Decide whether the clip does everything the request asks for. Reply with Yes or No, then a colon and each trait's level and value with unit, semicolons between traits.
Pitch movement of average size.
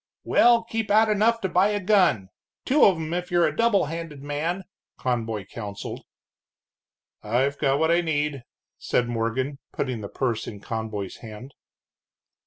No: wide, 8.6 semitones